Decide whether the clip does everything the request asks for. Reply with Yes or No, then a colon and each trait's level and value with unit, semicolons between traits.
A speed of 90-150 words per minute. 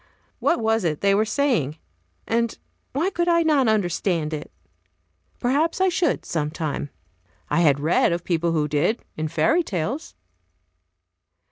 Yes: average, 140 wpm